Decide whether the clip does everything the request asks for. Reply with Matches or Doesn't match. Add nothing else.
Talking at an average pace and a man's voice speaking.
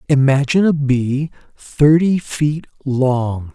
Doesn't match